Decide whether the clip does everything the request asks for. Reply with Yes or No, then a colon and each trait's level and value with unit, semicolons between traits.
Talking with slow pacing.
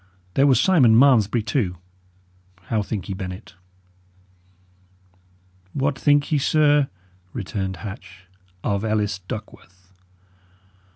Yes: slow, 100 wpm